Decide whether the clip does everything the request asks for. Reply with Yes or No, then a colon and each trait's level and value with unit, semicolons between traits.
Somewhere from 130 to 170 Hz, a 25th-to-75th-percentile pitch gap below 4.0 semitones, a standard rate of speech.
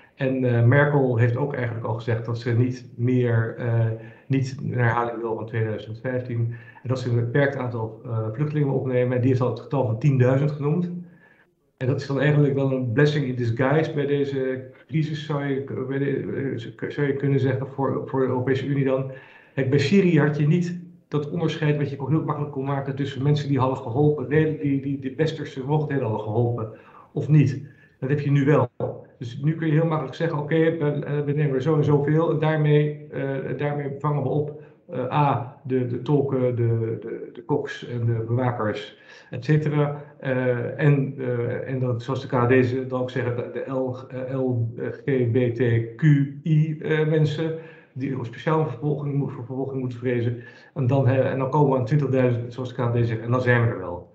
No: low, 135 Hz; average, 2.9 semitones; fast, 205 wpm